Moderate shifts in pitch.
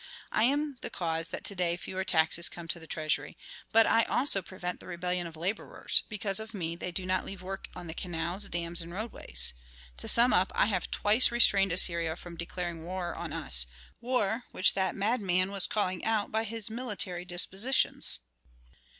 Yes: average, 3.8 semitones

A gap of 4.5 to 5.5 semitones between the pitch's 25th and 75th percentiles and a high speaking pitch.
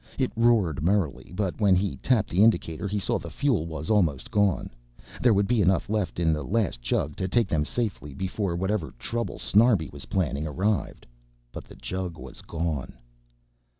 No: average, 4.9 semitones; very low, 95 Hz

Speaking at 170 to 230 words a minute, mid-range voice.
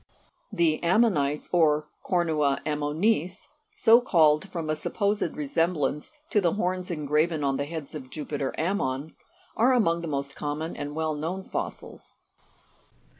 No: average, 155 wpm; medium, 160 Hz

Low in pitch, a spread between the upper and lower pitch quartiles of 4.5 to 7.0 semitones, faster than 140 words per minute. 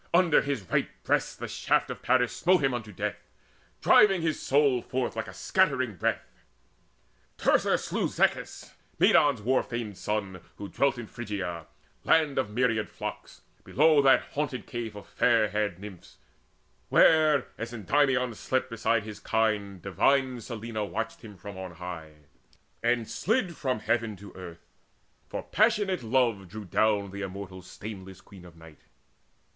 Yes: low, 110 Hz; average, 4.8 semitones; average, 150 wpm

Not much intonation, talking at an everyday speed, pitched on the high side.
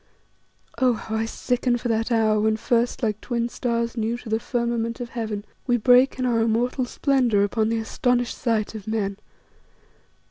Yes: narrow, 1.8 semitones; average, 175 wpm; high, 230 Hz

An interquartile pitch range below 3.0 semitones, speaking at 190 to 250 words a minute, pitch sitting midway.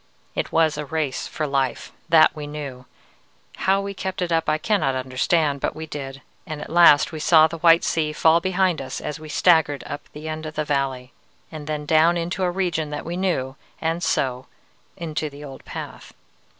Yes: narrow, 2.6 semitones; average, 200 wpm; medium, 155 Hz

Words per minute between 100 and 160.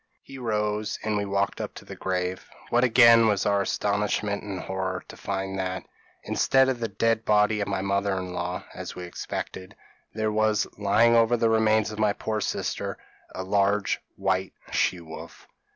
No: average, 185 wpm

